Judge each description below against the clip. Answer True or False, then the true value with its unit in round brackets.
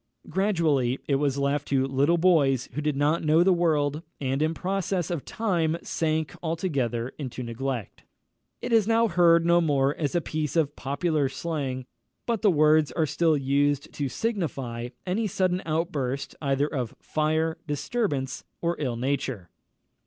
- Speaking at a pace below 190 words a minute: True (155 wpm)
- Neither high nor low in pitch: True (150 Hz)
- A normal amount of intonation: True (3.8 semitones)